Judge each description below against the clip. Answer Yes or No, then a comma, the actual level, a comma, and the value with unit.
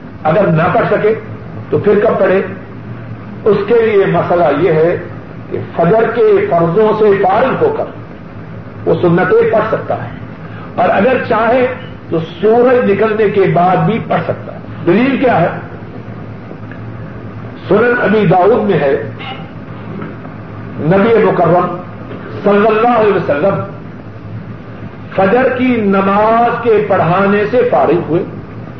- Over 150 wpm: No, average, 125 wpm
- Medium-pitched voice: No, high, 195 Hz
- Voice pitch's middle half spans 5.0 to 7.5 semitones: Yes, wide, 5.4 semitones